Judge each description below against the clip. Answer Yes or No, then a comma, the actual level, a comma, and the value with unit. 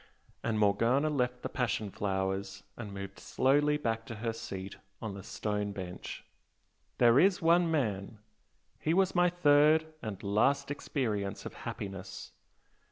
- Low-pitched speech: Yes, low, 115 Hz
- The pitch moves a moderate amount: No, wide, 6.6 semitones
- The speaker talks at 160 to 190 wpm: No, average, 140 wpm